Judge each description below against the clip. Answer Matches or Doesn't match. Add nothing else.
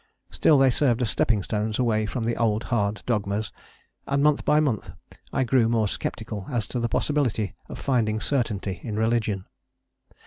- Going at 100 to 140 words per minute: Doesn't match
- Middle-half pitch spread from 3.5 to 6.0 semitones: Doesn't match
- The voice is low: Matches